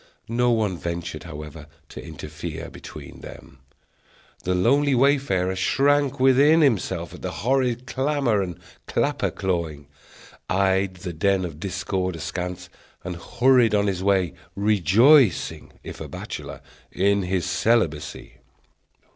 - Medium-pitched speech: No, very low, 95 Hz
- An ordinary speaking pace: No, slow, 120 wpm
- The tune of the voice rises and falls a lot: Yes, wide, 6.0 semitones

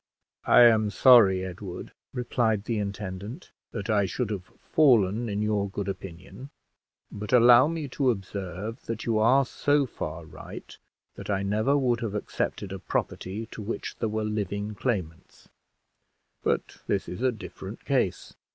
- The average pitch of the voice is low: Yes, low, 105 Hz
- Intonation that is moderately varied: Yes, average, 3.6 semitones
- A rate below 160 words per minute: Yes, average, 150 wpm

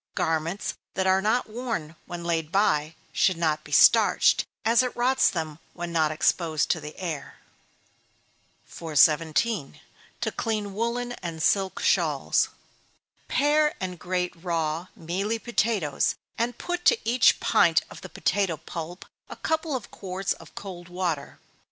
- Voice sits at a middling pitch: Yes, medium, 180 Hz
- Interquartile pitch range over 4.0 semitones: Yes, wide, 5.6 semitones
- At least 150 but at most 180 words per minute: No, average, 140 wpm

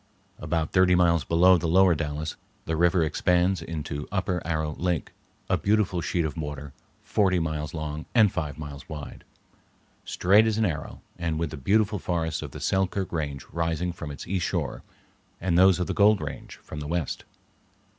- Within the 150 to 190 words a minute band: Yes, average, 175 wpm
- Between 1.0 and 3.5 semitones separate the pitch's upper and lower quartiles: Yes, average, 3.2 semitones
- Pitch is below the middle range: Yes, very low, 85 Hz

